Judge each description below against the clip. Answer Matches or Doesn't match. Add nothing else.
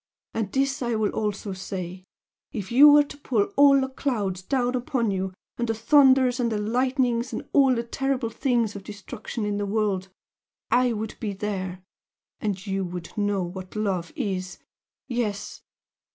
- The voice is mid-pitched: Doesn't match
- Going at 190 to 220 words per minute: Doesn't match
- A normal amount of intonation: Matches